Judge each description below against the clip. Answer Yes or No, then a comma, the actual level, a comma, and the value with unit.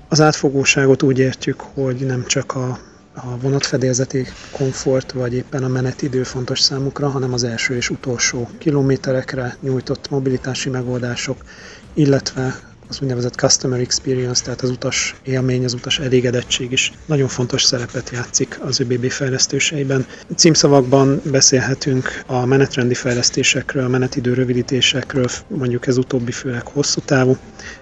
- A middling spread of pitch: No, narrow, 1.5 semitones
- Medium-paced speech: Yes, average, 130 wpm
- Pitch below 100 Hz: No, low, 130 Hz